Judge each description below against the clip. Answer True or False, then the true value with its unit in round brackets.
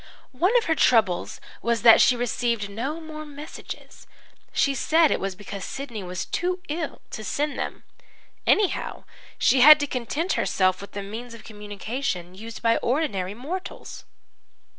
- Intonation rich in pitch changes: True (6.6 semitones)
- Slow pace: False (155 wpm)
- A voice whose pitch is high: True (240 Hz)